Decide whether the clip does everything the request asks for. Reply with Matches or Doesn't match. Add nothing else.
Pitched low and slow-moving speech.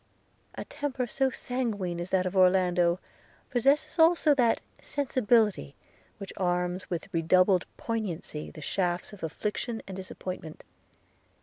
Doesn't match